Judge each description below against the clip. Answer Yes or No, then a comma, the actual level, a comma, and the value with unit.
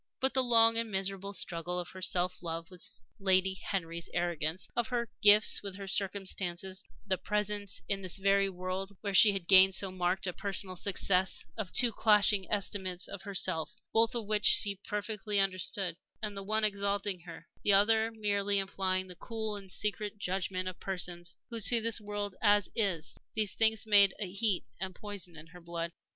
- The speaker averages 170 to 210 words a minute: Yes, average, 180 wpm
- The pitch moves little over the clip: Yes, narrow, 2.2 semitones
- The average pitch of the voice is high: Yes, high, 195 Hz